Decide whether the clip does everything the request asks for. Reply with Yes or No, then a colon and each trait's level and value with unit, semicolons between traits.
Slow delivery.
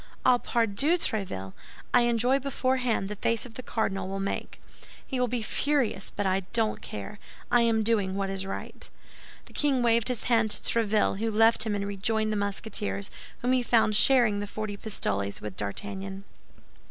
No: average, 175 wpm